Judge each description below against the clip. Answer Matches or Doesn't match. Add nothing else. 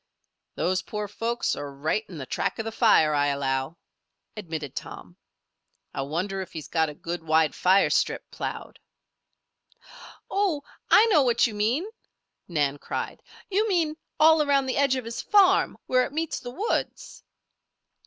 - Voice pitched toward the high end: Matches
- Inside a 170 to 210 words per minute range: Doesn't match